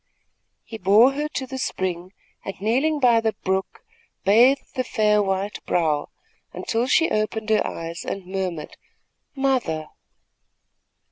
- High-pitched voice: Yes, high, 215 Hz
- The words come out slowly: Yes, slow, 130 wpm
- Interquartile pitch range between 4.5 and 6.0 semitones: Yes, average, 5.2 semitones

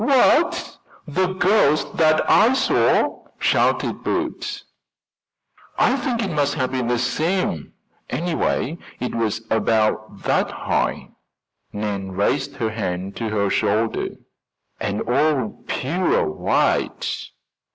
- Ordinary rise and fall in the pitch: No, wide, 8.1 semitones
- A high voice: No, low, 130 Hz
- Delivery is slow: Yes, slow, 110 wpm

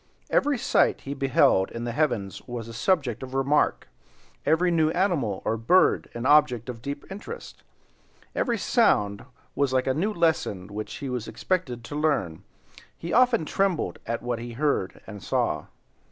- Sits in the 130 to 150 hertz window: Yes, low, 135 Hz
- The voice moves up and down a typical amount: No, wide, 6.3 semitones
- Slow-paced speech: No, average, 170 wpm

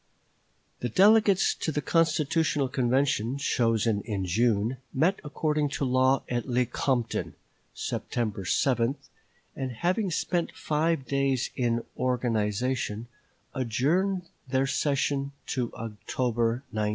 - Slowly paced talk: Yes, slow, 110 wpm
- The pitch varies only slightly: No, average, 4.1 semitones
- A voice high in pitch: No, low, 130 Hz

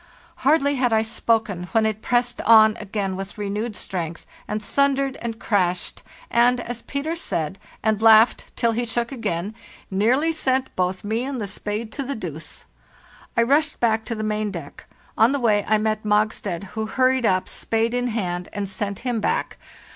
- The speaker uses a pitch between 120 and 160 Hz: No, high, 220 Hz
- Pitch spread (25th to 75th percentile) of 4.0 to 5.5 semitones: No, average, 3.2 semitones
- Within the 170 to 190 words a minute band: Yes, average, 175 wpm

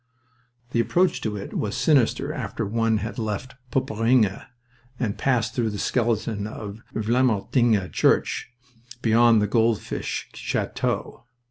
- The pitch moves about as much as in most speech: No, narrow, 2.2 semitones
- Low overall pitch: Yes, low, 115 Hz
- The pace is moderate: No, slow, 115 wpm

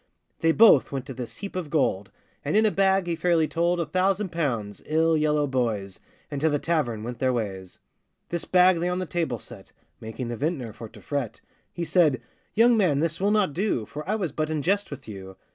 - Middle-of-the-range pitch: Yes, medium, 155 Hz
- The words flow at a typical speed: No, fast, 220 wpm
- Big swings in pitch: Yes, wide, 6.3 semitones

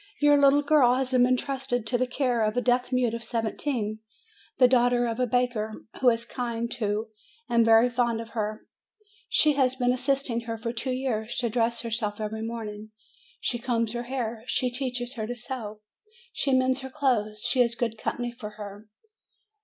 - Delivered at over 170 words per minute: Yes, average, 185 wpm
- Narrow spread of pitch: Yes, narrow, 2.2 semitones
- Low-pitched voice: No, high, 240 Hz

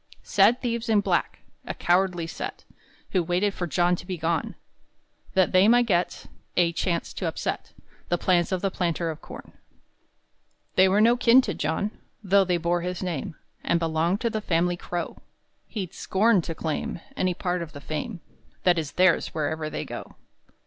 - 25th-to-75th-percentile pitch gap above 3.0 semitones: No, average, 2.7 semitones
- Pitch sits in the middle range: Yes, medium, 180 Hz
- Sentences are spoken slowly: No, average, 175 wpm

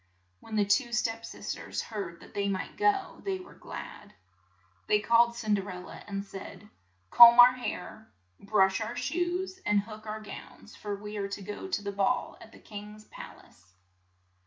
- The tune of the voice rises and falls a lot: No, average, 2.9 semitones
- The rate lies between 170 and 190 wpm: Yes, average, 185 wpm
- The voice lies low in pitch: No, high, 215 Hz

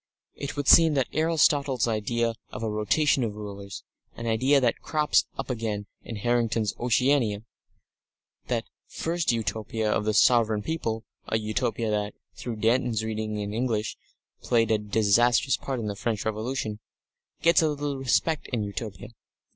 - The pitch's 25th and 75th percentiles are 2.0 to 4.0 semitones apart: Yes, average, 3.6 semitones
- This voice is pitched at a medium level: No, low, 115 Hz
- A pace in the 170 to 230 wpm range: No, average, 150 wpm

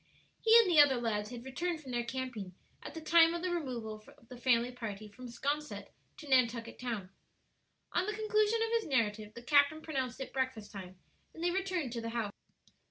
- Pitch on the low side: No, very high, 255 Hz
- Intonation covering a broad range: Yes, wide, 6.0 semitones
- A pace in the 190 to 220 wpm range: Yes, average, 200 wpm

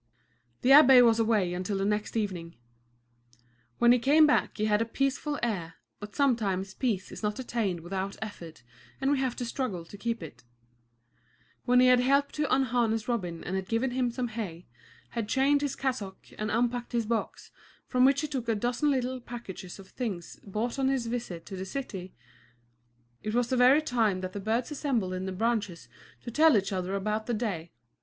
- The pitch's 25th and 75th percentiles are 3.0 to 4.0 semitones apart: No, average, 4.6 semitones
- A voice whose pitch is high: Yes, high, 230 Hz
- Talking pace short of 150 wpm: No, average, 195 wpm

